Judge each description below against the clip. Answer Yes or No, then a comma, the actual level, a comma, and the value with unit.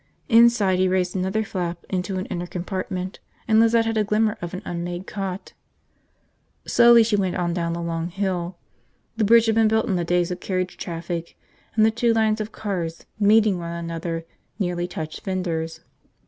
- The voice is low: No, medium, 185 Hz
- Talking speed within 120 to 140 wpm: No, average, 180 wpm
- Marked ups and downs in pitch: No, average, 3.8 semitones